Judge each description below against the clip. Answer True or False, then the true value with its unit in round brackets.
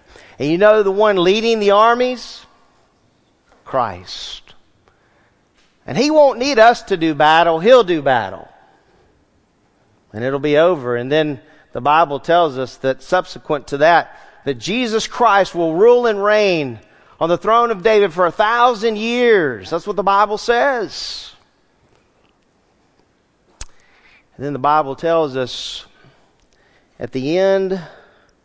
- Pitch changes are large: True (7.4 semitones)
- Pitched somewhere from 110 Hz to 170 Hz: False (180 Hz)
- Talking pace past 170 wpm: False (135 wpm)